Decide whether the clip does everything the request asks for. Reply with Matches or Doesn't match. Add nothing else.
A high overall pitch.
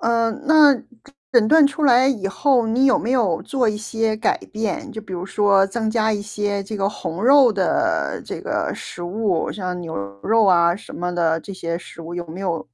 Matches